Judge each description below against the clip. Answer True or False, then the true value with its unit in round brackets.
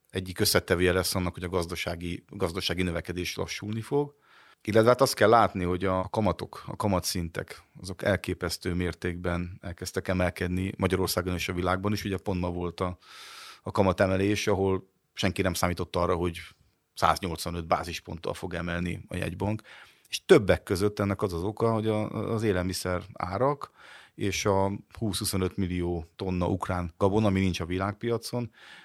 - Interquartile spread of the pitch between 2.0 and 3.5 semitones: True (2.4 semitones)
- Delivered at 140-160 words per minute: True (150 wpm)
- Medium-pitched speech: False (95 Hz)